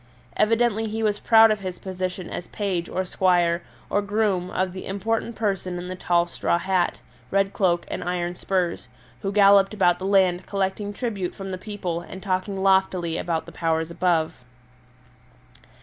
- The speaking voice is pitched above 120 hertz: Yes, high, 190 Hz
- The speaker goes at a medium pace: Yes, average, 165 wpm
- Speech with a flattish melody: Yes, narrow, 2.3 semitones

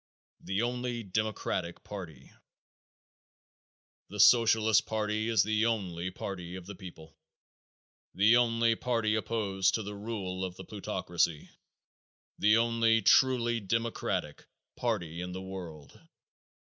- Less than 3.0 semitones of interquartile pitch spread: No, average, 3.7 semitones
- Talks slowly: Yes, slow, 115 wpm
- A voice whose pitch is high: No, low, 105 Hz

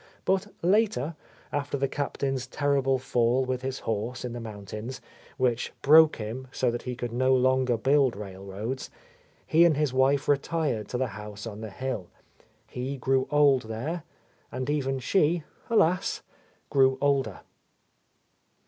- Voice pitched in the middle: No, low, 130 Hz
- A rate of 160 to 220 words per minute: No, average, 150 wpm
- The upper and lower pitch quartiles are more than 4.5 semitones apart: No, average, 3.2 semitones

